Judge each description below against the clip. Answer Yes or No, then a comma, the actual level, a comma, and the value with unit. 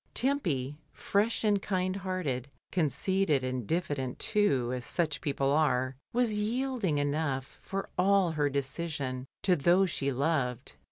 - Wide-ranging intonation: Yes, wide, 6.2 semitones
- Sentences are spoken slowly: Yes, slow, 130 wpm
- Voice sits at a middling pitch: Yes, medium, 155 Hz